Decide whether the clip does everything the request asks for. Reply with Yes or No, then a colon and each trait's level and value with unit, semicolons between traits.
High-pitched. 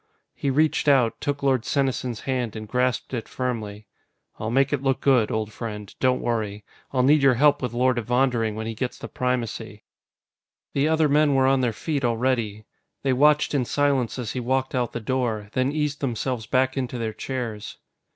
No: low, 125 Hz